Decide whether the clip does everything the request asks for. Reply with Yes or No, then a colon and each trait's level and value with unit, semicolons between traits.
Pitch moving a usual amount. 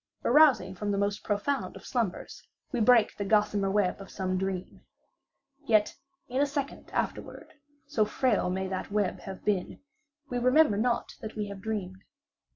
Yes: average, 3.9 semitones